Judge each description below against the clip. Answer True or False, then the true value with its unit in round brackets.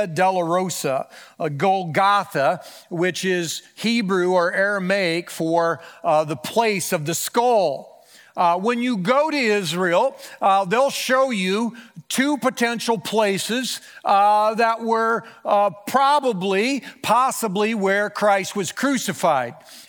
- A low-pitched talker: False (205 Hz)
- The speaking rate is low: True (110 wpm)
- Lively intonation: False (4.4 semitones)